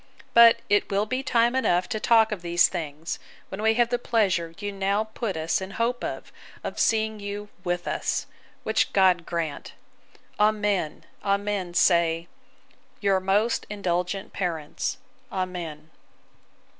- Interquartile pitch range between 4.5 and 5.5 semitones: No, average, 3.8 semitones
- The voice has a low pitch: No, high, 195 Hz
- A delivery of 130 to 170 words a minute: Yes, average, 140 wpm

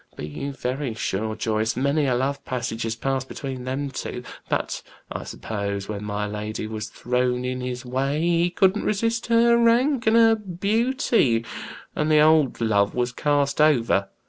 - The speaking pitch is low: Yes, low, 130 Hz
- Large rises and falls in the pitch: Yes, wide, 6.7 semitones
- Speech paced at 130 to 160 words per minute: No, average, 170 wpm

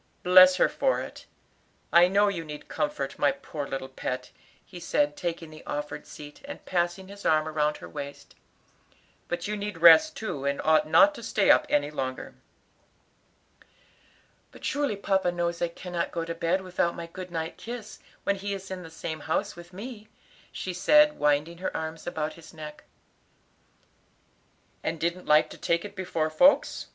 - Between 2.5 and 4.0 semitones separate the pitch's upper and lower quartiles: Yes, average, 3.7 semitones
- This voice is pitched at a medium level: Yes, medium, 170 Hz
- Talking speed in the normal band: Yes, average, 175 wpm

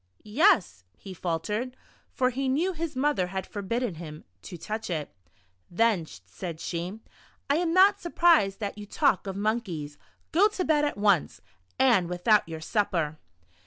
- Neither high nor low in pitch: No, high, 210 Hz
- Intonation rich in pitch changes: Yes, wide, 7.9 semitones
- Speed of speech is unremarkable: Yes, average, 155 wpm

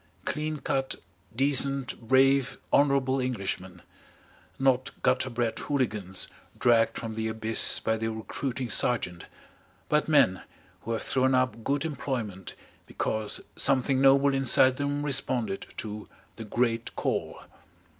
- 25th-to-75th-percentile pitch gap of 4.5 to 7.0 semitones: No, average, 3.5 semitones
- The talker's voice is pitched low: Yes, low, 125 Hz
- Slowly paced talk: Yes, slow, 120 wpm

